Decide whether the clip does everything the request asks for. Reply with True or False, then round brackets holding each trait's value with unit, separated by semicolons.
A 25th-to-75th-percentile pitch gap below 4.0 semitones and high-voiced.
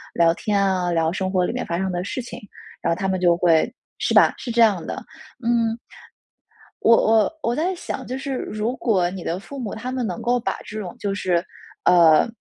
False (4.8 semitones; 195 Hz)